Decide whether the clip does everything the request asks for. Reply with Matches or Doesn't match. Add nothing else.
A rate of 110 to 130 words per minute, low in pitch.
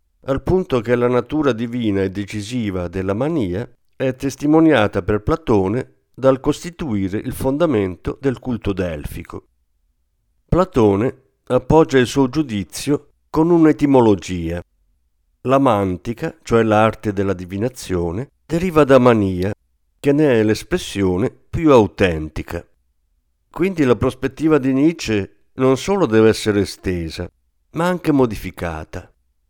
Matches